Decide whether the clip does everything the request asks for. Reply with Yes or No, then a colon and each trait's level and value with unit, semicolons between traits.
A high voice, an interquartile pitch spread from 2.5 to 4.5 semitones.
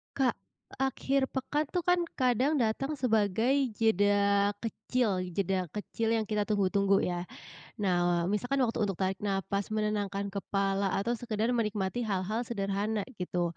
Yes: high, 210 Hz; average, 3.2 semitones